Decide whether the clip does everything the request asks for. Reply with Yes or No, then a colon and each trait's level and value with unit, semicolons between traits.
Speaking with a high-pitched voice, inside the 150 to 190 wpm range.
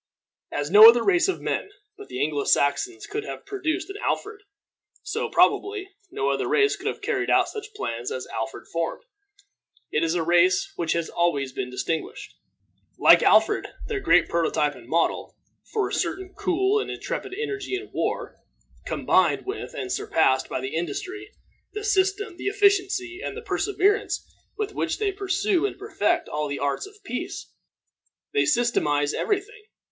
Yes: very high, 370 Hz; average, 165 wpm